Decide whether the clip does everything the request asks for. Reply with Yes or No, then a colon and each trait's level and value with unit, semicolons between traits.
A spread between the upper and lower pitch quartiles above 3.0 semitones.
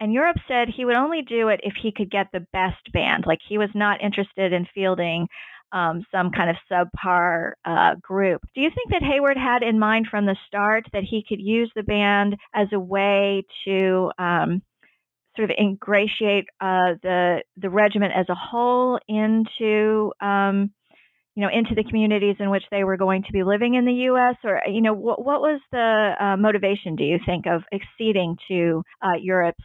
No: average, 2.7 semitones